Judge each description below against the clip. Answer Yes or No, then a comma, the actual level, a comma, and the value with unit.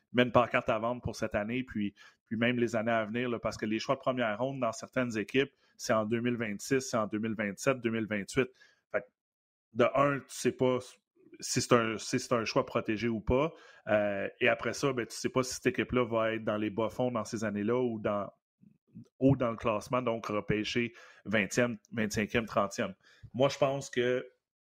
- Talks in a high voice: No, low, 115 Hz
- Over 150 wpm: Yes, average, 205 wpm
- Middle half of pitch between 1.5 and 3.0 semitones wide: Yes, narrow, 2.4 semitones